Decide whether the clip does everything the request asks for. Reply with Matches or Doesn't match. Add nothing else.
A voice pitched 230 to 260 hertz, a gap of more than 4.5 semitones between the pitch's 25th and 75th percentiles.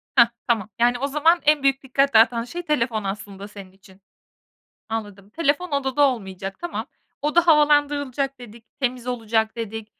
Matches